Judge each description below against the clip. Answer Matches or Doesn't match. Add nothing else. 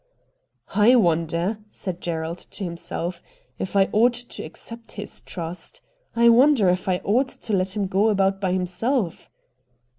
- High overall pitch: Matches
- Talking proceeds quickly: Doesn't match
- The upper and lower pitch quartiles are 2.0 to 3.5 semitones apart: Doesn't match